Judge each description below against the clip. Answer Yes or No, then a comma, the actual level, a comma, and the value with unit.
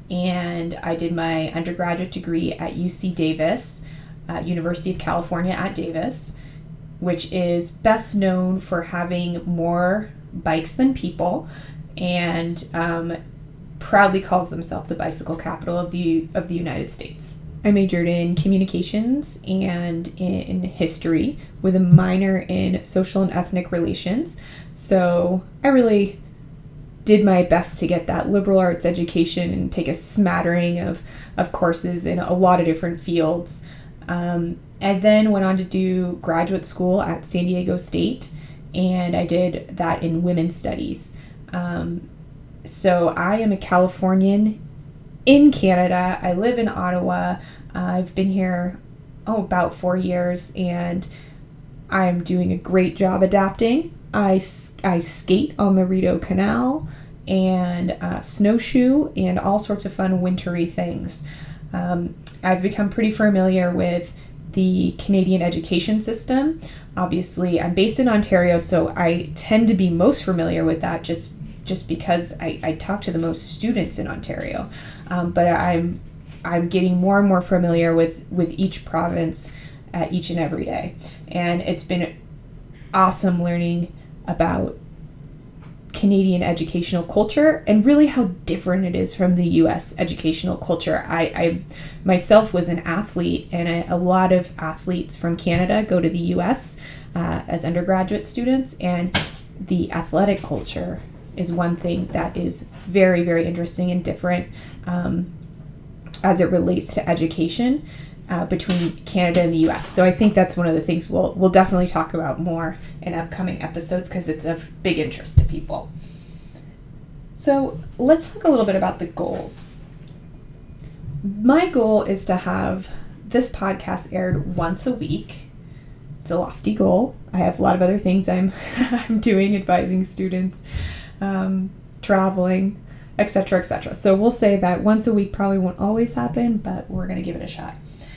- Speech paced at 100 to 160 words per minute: Yes, average, 150 wpm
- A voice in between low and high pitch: Yes, medium, 175 Hz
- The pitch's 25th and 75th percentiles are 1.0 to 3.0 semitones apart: Yes, average, 2.7 semitones